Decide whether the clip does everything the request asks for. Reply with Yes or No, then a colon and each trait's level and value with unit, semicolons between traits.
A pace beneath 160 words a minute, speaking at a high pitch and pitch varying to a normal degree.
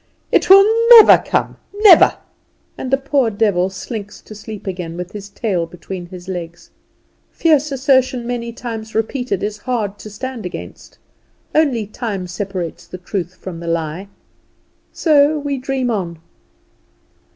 No: average, 140 wpm; high, 210 Hz; wide, 6.1 semitones